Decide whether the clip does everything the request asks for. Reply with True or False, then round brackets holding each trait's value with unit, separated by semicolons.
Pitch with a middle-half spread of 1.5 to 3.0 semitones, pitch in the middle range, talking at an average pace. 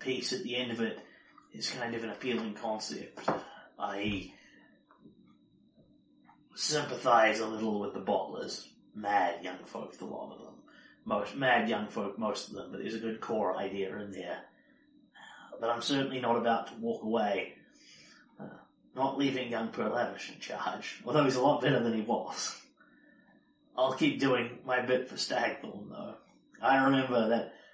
False (2.4 semitones; 115 Hz; 165 wpm)